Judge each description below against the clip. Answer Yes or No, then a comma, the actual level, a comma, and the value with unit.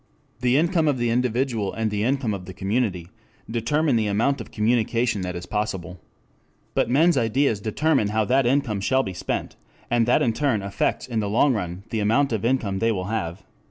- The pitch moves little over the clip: No, average, 4.1 semitones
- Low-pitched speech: Yes, low, 115 Hz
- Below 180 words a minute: No, average, 195 wpm